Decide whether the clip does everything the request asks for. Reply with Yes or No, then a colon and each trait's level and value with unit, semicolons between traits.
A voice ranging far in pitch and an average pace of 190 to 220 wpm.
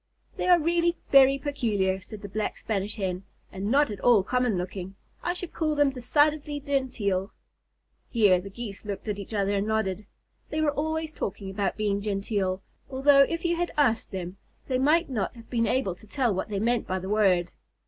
Yes: wide, 6.3 semitones; average, 195 wpm